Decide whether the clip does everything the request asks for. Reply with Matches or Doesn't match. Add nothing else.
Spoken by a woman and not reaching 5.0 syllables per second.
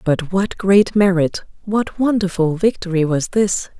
Matches